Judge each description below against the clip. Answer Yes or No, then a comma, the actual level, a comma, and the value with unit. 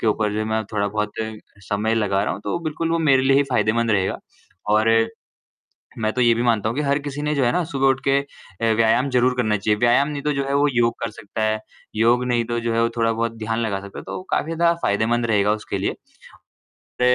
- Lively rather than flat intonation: No, average, 3.9 semitones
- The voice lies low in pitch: Yes, low, 115 Hz